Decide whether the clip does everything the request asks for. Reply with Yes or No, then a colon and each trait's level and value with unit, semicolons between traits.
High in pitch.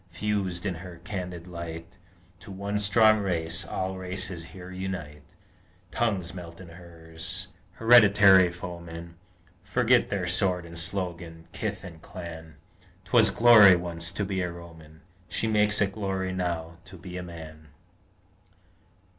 No: very low, 90 Hz